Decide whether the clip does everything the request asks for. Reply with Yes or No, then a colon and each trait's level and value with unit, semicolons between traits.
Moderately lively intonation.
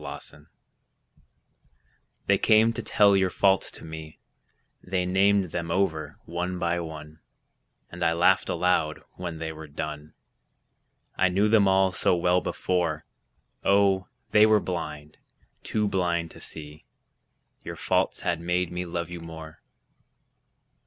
Yes: average, 3.1 semitones